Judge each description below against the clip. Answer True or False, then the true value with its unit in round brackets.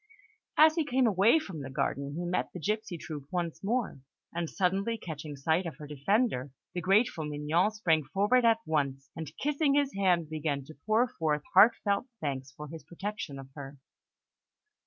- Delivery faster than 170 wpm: True (180 wpm)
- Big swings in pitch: True (6.4 semitones)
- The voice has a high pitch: False (170 Hz)